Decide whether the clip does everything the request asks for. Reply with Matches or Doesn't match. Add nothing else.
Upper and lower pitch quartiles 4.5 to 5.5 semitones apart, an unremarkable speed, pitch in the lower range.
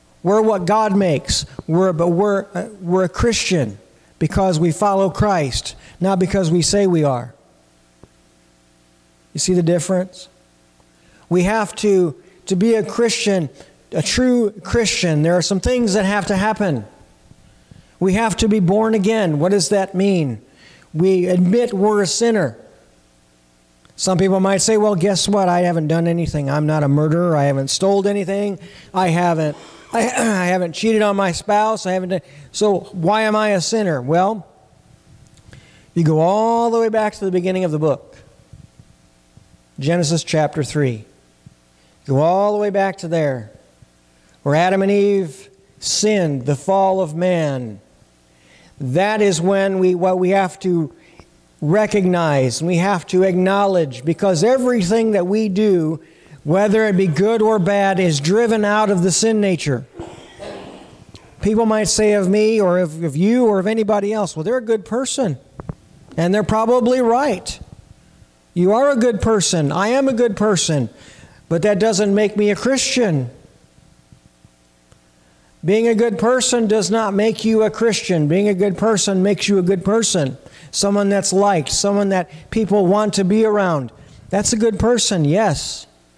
Doesn't match